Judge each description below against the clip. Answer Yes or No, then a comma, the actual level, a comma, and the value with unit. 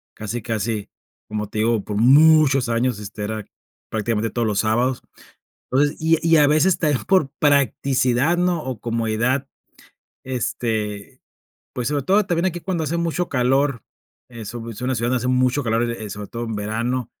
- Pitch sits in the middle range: No, low, 125 Hz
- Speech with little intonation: No, average, 4.6 semitones